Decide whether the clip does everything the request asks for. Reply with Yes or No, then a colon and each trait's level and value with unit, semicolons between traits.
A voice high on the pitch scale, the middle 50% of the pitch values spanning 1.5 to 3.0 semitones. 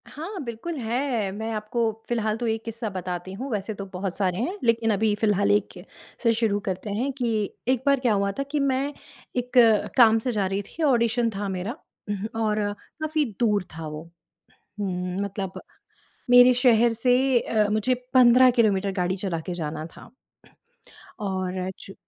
No: high, 220 Hz; average, 4.1 semitones